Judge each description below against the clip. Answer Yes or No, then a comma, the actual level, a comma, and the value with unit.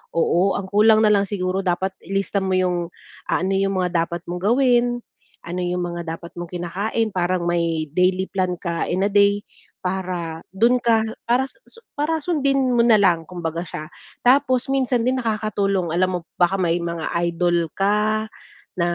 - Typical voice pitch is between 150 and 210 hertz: Yes, high, 190 Hz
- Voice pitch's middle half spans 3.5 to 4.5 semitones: Yes, average, 4.0 semitones